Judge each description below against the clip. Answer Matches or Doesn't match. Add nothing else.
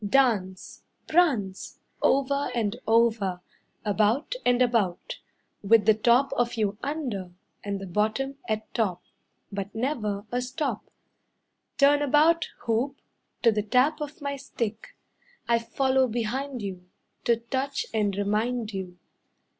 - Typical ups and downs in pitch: Matches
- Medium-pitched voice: Doesn't match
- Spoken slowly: Matches